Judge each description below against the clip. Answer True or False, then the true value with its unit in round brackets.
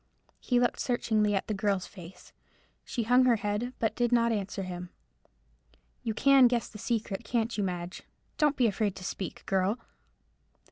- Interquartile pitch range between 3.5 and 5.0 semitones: True (3.8 semitones)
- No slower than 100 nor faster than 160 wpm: False (170 wpm)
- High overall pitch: True (215 Hz)